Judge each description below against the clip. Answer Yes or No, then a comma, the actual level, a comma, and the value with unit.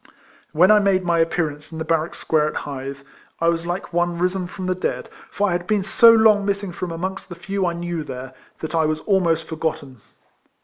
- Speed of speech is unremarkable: No, fast, 225 wpm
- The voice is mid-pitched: Yes, medium, 175 Hz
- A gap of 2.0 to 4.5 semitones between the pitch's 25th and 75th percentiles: Yes, average, 2.9 semitones